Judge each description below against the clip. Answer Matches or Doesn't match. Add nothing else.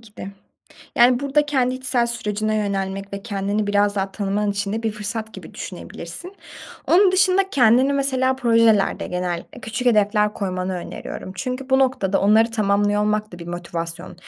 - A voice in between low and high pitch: Doesn't match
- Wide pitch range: Doesn't match